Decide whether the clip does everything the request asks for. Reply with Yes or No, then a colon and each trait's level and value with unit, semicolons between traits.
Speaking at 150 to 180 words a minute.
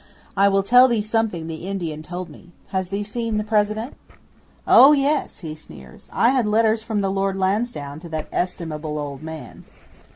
Yes: average, 175 wpm